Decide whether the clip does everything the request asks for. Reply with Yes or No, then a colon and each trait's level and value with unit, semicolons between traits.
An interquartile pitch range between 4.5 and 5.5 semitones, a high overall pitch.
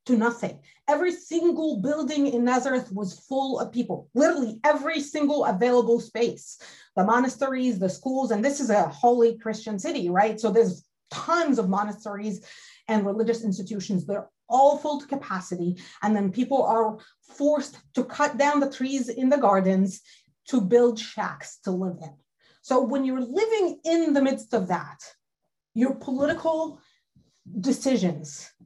Yes: average, 5.2 semitones; high, 245 Hz